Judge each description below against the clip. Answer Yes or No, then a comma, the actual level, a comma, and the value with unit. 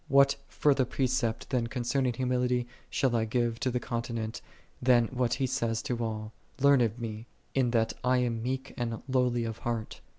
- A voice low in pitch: Yes, low, 120 Hz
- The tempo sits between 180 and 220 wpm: Yes, average, 185 wpm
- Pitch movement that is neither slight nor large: No, narrow, 1.9 semitones